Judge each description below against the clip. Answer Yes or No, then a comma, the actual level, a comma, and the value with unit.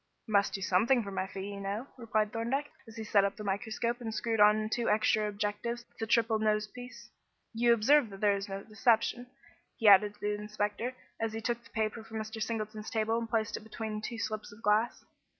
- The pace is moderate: No, fast, 220 wpm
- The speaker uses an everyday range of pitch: No, narrow, 1.8 semitones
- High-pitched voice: Yes, high, 220 Hz